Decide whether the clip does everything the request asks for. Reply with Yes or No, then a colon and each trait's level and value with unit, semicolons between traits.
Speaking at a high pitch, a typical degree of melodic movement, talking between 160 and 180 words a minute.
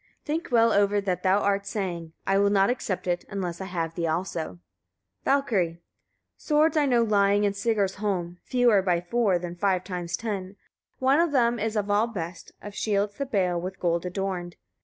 No: high, 200 Hz; average, 4.0 semitones; average, 190 wpm